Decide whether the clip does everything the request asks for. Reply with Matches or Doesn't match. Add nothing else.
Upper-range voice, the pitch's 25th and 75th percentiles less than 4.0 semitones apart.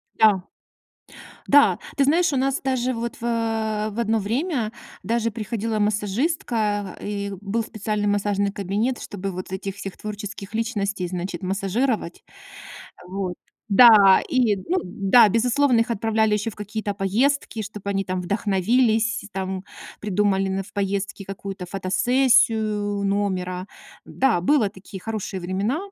Matches